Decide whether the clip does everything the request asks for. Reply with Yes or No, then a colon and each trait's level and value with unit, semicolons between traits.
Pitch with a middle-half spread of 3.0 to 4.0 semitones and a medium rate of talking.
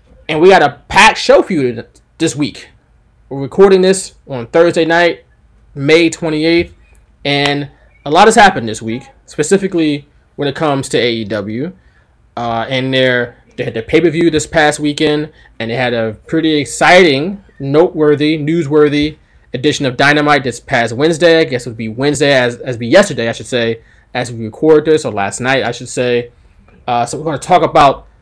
No: average, 4.8 semitones; average, 180 wpm